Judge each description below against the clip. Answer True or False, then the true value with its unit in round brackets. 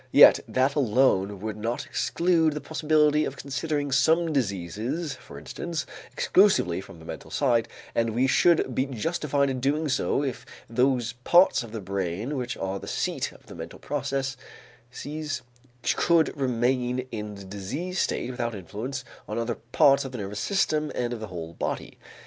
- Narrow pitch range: False (5.2 semitones)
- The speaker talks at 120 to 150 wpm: False (165 wpm)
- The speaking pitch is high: False (130 Hz)